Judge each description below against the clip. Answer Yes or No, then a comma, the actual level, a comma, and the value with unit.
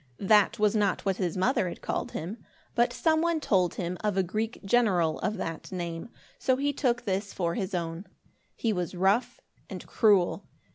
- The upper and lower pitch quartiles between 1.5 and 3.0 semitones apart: No, average, 4.7 semitones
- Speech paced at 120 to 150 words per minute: No, average, 185 wpm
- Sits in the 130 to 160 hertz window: No, high, 195 Hz